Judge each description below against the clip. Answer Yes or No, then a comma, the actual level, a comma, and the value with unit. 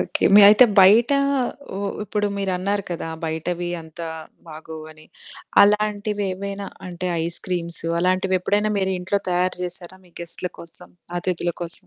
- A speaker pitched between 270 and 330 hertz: No, medium, 185 Hz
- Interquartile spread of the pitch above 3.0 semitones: No, average, 2.7 semitones